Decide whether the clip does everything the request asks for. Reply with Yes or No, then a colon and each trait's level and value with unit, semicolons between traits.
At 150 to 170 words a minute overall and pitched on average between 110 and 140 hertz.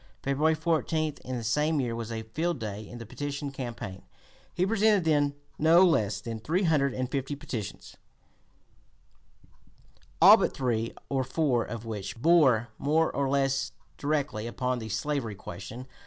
Yes: average, 155 wpm; low, 135 Hz